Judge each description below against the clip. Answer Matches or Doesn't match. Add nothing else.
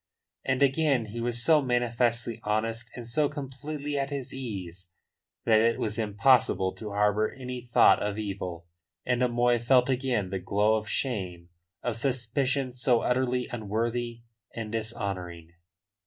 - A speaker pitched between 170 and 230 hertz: Doesn't match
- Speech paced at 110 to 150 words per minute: Matches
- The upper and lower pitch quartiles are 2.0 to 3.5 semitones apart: Matches